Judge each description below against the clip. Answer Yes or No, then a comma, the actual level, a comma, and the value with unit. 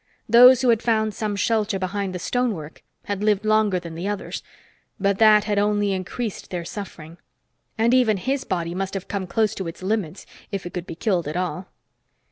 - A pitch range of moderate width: Yes, average, 3.0 semitones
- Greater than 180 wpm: Yes, average, 195 wpm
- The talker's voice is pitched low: No, high, 200 Hz